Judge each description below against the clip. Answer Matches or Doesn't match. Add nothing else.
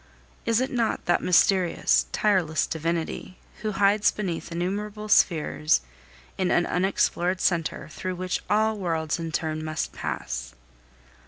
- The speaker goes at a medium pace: Doesn't match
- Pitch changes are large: Doesn't match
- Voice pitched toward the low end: Doesn't match